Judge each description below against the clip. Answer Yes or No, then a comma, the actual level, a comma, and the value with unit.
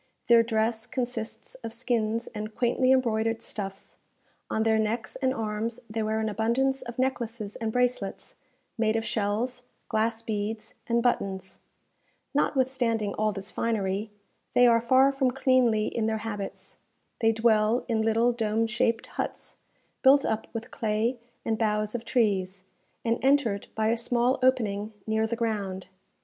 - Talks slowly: No, average, 150 wpm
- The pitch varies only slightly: Yes, narrow, 2.0 semitones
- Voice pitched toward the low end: No, high, 225 Hz